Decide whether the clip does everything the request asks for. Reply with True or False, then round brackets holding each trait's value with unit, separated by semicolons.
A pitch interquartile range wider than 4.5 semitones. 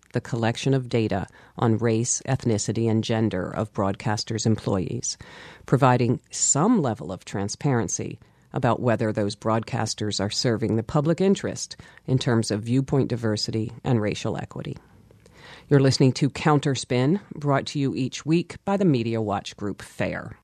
False (3.6 semitones)